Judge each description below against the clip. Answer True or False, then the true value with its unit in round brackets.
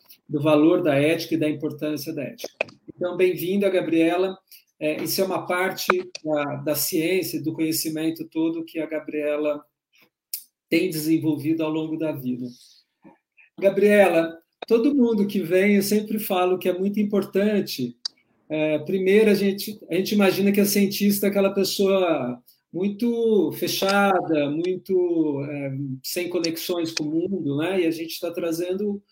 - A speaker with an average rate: True (150 wpm)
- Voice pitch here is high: False (175 Hz)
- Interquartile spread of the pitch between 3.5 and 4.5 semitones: True (3.8 semitones)